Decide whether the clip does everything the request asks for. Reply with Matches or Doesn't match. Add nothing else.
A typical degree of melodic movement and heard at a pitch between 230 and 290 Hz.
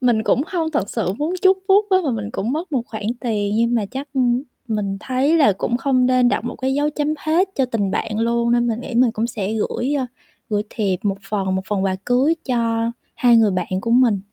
Matches